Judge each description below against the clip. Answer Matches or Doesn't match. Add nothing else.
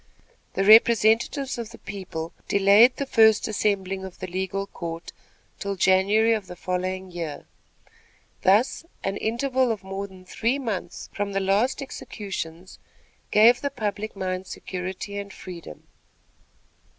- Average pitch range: Matches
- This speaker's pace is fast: Doesn't match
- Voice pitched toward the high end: Matches